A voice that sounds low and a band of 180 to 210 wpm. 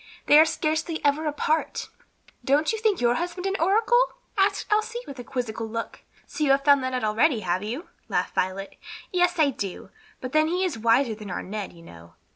No: very high, 280 Hz; fast, 205 wpm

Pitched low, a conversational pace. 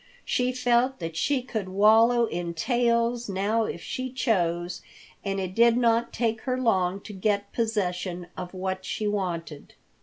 No: high, 210 Hz; average, 155 wpm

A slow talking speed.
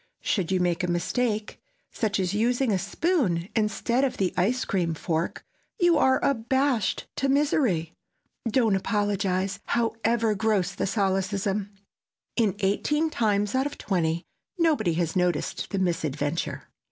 Yes: slow, 130 wpm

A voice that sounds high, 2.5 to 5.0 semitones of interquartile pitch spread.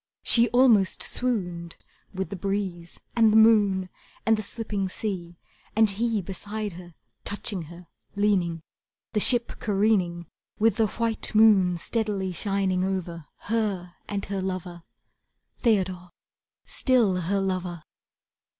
Yes: high, 195 Hz; average, 3.2 semitones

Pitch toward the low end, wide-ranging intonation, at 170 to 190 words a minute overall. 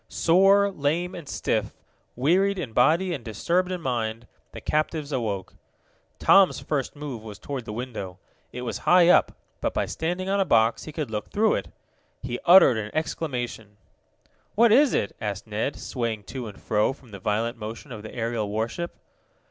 Yes: low, 130 Hz; wide, 7.6 semitones; average, 175 wpm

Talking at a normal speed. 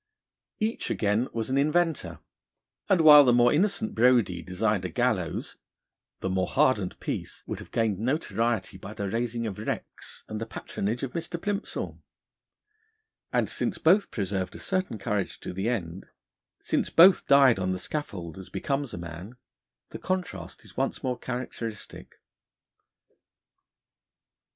Yes: average, 145 wpm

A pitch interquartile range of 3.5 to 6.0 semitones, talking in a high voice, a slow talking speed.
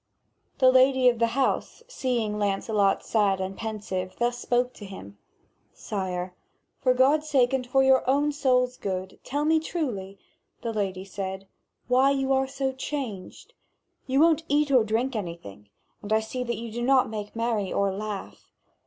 No: average, 4.9 semitones; high, 235 Hz; average, 165 wpm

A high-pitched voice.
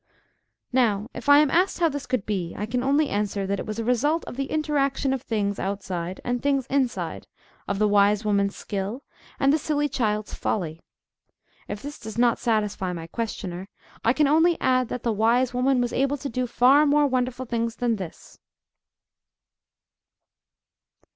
Yes: high, 240 Hz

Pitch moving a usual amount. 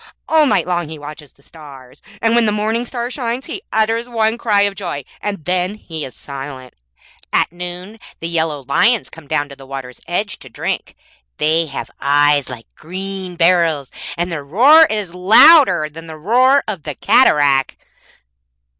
No: wide, 6.8 semitones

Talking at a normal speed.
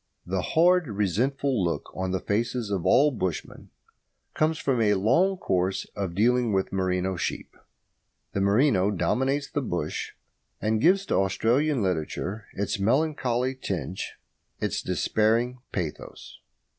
No: slow, 130 wpm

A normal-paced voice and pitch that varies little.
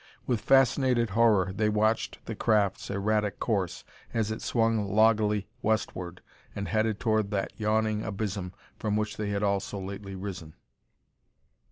Yes: average, 145 wpm; narrow, 1.7 semitones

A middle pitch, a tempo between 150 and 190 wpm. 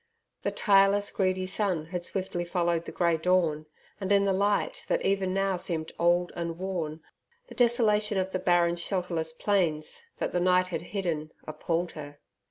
Yes: medium, 180 Hz; average, 170 wpm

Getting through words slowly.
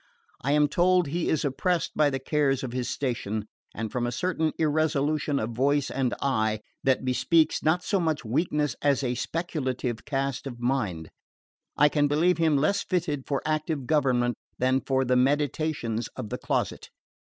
No: average, 170 wpm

